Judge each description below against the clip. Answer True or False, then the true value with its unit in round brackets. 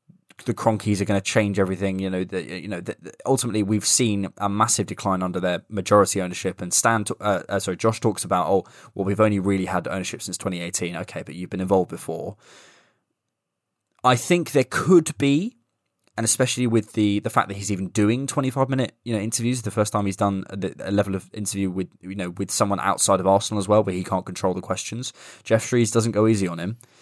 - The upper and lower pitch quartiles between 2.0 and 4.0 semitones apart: True (3.1 semitones)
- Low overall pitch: True (105 Hz)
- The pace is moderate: False (220 wpm)